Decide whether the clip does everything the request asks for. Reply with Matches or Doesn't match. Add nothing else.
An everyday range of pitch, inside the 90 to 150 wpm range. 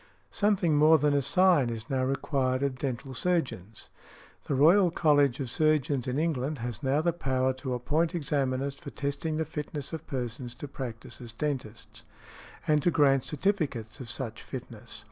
Doesn't match